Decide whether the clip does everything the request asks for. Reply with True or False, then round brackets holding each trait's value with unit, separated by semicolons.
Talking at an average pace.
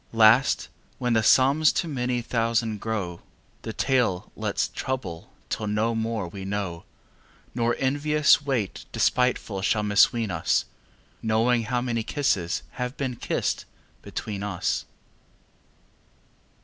False (125 wpm)